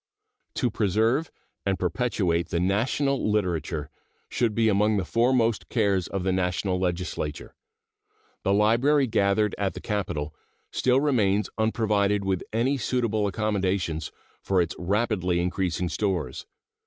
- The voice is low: Yes, low, 100 Hz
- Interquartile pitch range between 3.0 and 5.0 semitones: Yes, average, 3.6 semitones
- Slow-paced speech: Yes, slow, 125 wpm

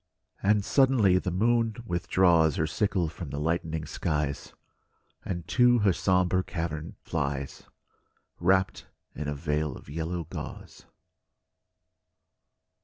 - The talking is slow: Yes, slow, 110 wpm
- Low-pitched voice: Yes, very low, 85 Hz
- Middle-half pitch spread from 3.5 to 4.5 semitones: Yes, average, 3.8 semitones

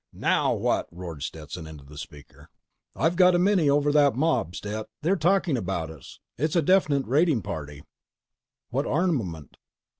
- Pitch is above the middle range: No, low, 130 Hz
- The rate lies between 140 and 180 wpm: Yes, average, 155 wpm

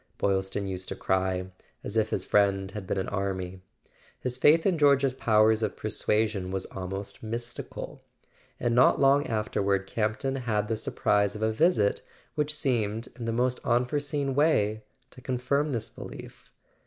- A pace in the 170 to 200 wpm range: No, average, 155 wpm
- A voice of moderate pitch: No, low, 110 Hz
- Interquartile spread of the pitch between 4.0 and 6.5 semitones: Yes, average, 4.5 semitones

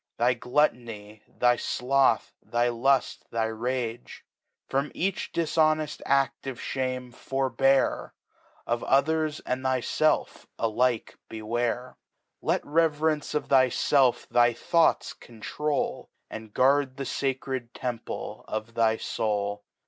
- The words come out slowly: Yes, slow, 110 wpm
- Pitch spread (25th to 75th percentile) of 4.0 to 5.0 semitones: No, average, 2.9 semitones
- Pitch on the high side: No, low, 130 Hz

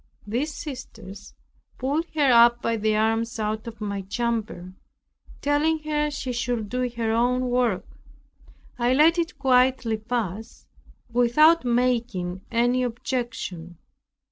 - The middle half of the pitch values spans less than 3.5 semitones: Yes, average, 2.8 semitones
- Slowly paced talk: Yes, slow, 115 wpm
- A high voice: Yes, high, 240 Hz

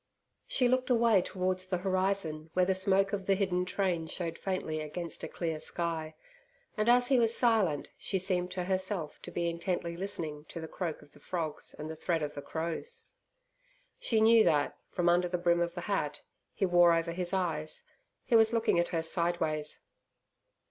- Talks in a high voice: No, medium, 180 Hz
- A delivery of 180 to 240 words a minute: Yes, average, 190 wpm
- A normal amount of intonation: Yes, average, 3.1 semitones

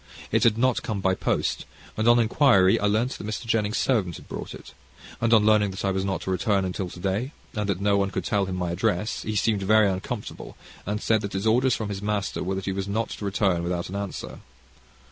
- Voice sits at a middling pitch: No, low, 100 Hz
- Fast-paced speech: Yes, fast, 240 wpm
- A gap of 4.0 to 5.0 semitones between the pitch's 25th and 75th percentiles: No, narrow, 2.4 semitones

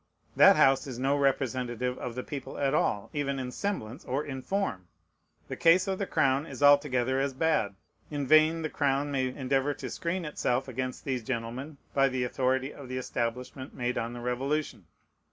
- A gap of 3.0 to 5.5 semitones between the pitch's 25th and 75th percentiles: No, narrow, 2.5 semitones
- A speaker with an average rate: Yes, average, 185 wpm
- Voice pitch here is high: No, low, 135 Hz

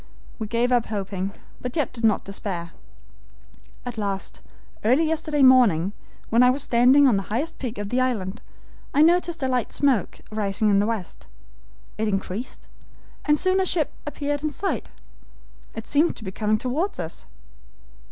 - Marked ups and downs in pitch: Yes, wide, 5.7 semitones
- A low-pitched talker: No, high, 240 Hz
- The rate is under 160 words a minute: No, average, 165 wpm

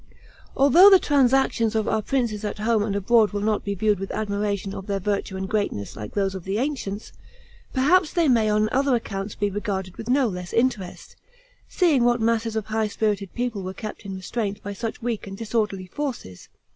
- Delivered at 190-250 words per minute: Yes, average, 195 wpm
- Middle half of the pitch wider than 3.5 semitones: No, average, 3.2 semitones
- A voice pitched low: No, high, 215 Hz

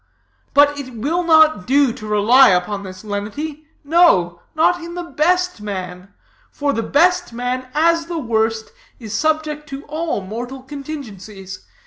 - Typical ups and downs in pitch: No, wide, 6.8 semitones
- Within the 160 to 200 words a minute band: No, average, 145 wpm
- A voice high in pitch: Yes, very high, 270 Hz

